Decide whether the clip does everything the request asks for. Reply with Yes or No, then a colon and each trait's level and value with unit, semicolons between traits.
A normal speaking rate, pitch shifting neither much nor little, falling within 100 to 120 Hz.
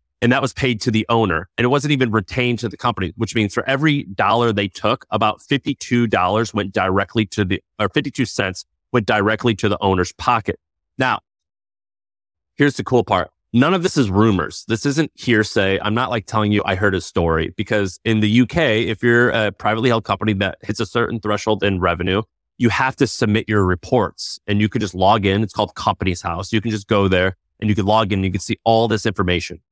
No: fast, 220 wpm; average, 3.4 semitones; low, 110 Hz